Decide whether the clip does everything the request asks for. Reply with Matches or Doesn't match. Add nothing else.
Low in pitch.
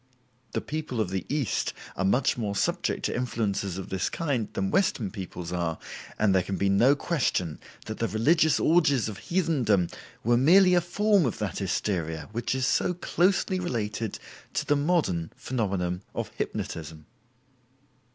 Matches